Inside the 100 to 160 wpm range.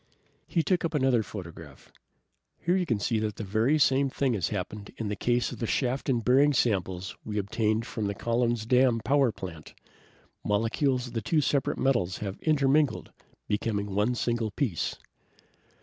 No: average, 175 wpm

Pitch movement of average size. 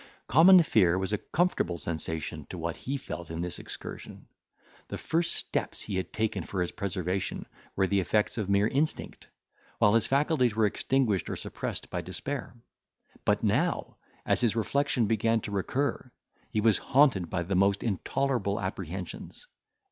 No: wide, 5.7 semitones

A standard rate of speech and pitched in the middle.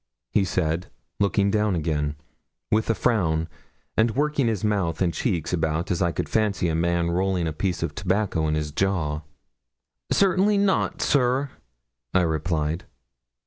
No: average, 150 wpm; very low, 90 Hz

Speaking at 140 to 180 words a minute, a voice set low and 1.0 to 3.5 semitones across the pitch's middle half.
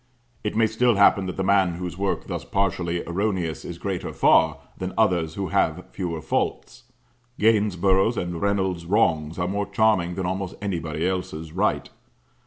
Yes: average, 160 wpm; very low, 95 Hz; average, 2.7 semitones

